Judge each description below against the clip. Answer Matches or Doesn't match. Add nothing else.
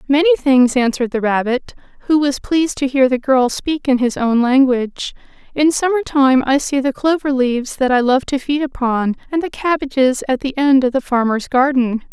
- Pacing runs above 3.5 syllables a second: Matches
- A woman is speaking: Matches